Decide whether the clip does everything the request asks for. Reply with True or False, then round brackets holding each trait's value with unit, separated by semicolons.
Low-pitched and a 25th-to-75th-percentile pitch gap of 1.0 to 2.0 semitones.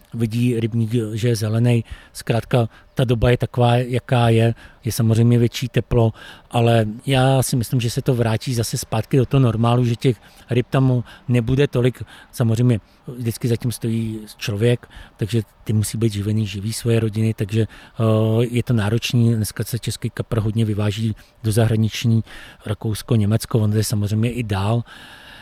True (115 Hz; 1.7 semitones)